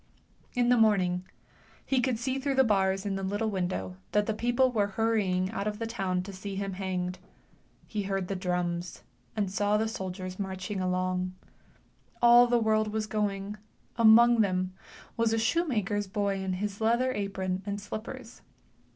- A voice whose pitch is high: Yes, high, 205 Hz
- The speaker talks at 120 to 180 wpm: Yes, average, 170 wpm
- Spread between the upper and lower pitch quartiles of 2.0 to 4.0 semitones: Yes, average, 3.1 semitones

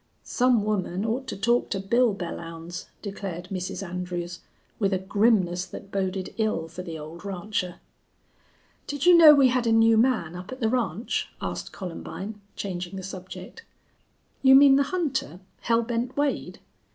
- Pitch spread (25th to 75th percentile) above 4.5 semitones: Yes, average, 5.1 semitones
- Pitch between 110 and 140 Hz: No, high, 200 Hz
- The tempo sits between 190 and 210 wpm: No, average, 160 wpm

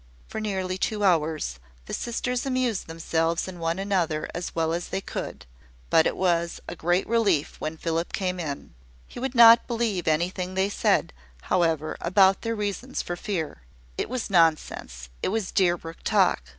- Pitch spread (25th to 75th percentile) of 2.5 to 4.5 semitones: Yes, average, 4.0 semitones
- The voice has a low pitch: No, medium, 180 Hz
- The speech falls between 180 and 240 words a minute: No, average, 165 wpm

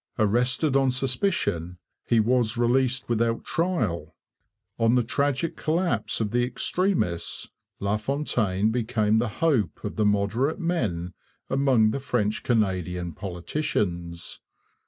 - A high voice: No, low, 115 Hz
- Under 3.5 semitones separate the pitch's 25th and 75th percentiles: No, average, 4.8 semitones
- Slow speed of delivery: Yes, slow, 115 wpm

